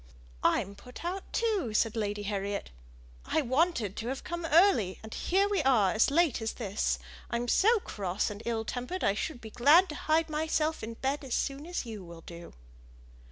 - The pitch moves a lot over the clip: Yes, wide, 7.3 semitones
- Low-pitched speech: No, very high, 250 Hz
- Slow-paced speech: No, average, 190 wpm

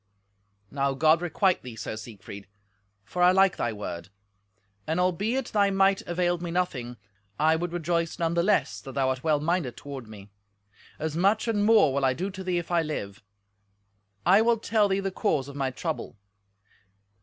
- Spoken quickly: No, average, 180 wpm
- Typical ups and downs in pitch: No, wide, 6.1 semitones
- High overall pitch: No, medium, 170 Hz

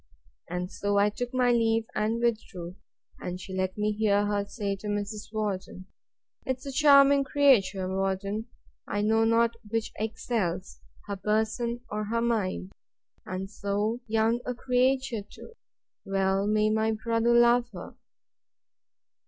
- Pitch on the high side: Yes, high, 215 Hz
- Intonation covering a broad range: No, average, 2.9 semitones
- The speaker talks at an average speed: No, slow, 130 wpm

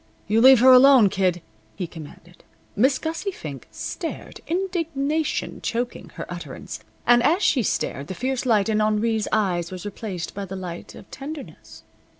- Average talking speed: Yes, average, 155 wpm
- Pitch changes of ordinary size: No, wide, 6.4 semitones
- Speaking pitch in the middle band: No, high, 225 Hz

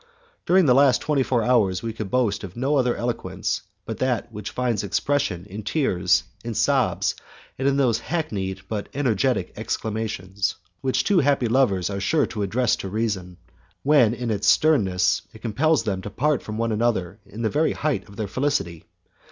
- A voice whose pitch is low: Yes, low, 115 Hz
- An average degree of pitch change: Yes, average, 5.0 semitones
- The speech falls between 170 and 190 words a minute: Yes, average, 180 wpm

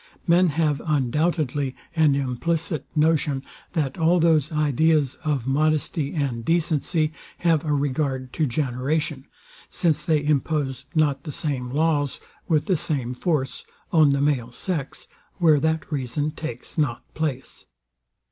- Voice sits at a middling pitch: Yes, medium, 150 Hz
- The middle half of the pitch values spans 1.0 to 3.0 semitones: Yes, average, 2.7 semitones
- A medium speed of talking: No, slow, 130 wpm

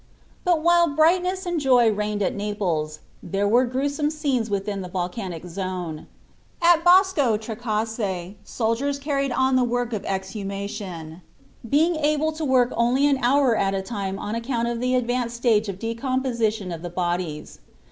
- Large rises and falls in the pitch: Yes, wide, 5.9 semitones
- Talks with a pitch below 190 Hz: No, high, 230 Hz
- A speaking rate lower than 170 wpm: Yes, average, 155 wpm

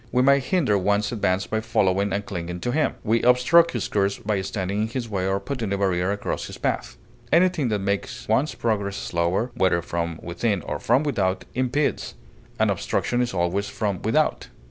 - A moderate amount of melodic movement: Yes, average, 4.4 semitones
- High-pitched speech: No, low, 105 Hz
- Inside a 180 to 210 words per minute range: Yes, average, 190 wpm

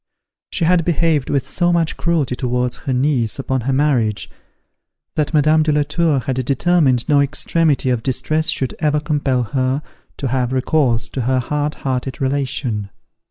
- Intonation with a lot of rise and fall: No, average, 3.2 semitones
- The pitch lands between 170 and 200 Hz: No, medium, 140 Hz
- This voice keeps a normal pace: Yes, average, 160 wpm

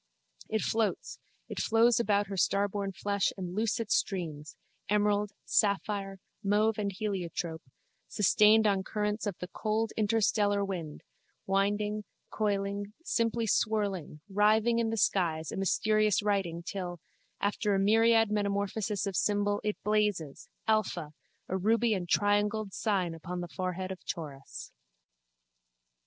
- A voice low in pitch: No, high, 205 Hz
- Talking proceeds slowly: Yes, slow, 130 wpm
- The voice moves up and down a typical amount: No, narrow, 2.1 semitones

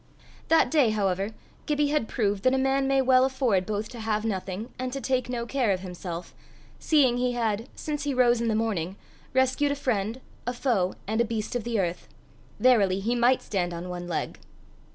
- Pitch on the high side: Yes, high, 235 Hz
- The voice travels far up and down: No, average, 4.8 semitones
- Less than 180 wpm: No, average, 200 wpm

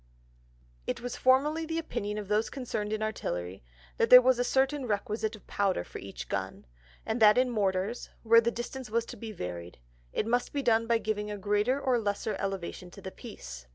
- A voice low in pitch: No, high, 220 Hz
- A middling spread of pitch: Yes, average, 3.5 semitones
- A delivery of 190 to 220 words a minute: Yes, fast, 205 wpm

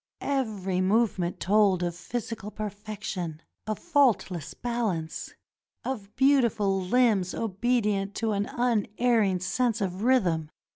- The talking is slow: Yes, slow, 105 wpm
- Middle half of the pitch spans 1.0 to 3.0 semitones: No, average, 4.1 semitones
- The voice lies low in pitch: No, high, 210 Hz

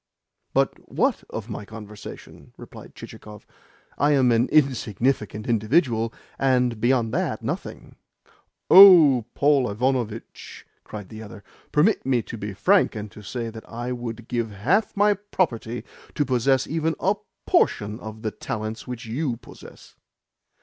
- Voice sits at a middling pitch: No, low, 120 Hz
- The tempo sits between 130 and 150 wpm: Yes, average, 140 wpm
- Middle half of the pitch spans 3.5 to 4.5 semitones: Yes, average, 4.2 semitones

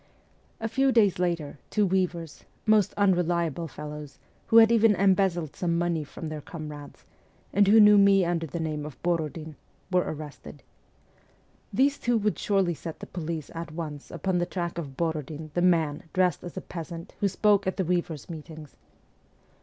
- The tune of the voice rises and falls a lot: No, average, 3.6 semitones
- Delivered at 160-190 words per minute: Yes, average, 170 wpm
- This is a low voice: No, medium, 170 Hz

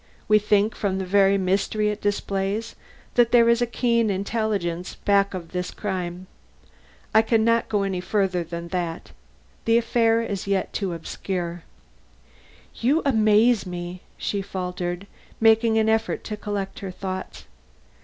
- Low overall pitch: No, high, 200 Hz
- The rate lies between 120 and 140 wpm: No, average, 150 wpm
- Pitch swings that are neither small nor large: Yes, average, 3.2 semitones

